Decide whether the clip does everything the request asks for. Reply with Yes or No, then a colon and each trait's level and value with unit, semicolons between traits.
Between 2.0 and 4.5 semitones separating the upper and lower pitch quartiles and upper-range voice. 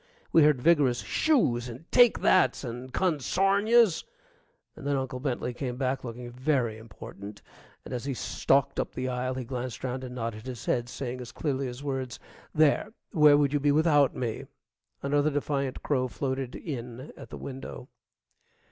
No: average, 2.9 semitones; low, 130 Hz